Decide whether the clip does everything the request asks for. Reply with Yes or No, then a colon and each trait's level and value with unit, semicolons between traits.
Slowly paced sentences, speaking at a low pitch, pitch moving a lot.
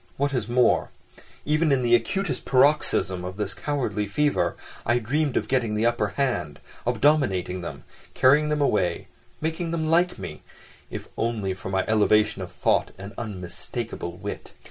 No: average, 155 wpm; low, 120 Hz; wide, 6.6 semitones